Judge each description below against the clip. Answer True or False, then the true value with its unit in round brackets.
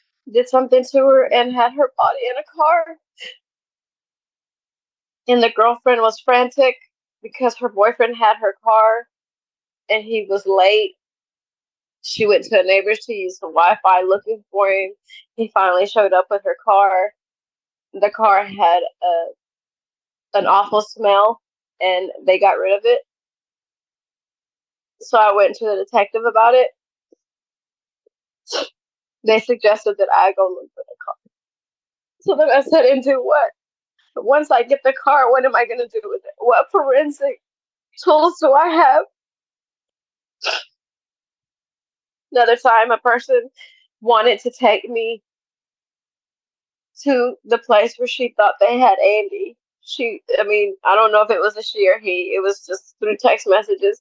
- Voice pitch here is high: True (235 Hz)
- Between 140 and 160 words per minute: True (150 wpm)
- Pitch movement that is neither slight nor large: False (6.0 semitones)